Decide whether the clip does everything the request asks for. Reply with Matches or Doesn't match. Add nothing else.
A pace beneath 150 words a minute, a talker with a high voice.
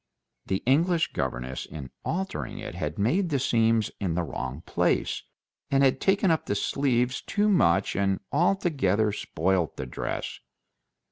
Doesn't match